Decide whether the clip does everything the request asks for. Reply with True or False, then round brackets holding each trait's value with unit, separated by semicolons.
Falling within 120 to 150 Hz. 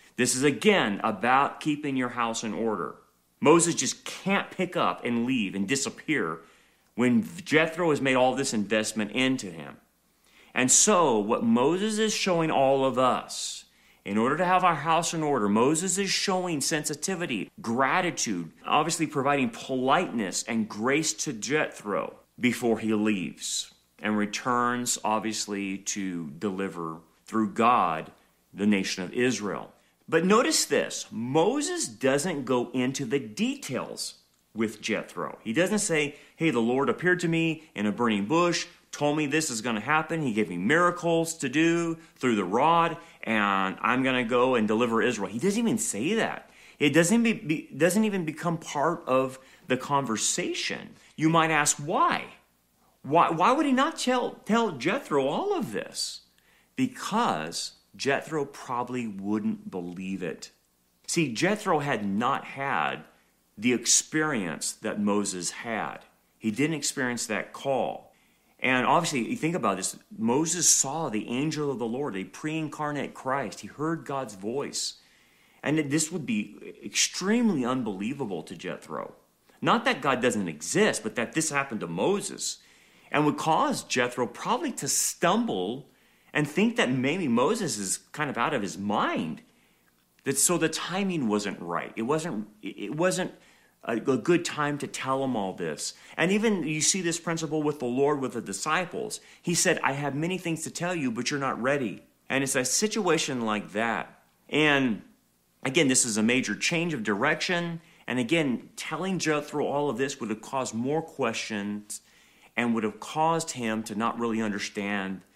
True (140 Hz)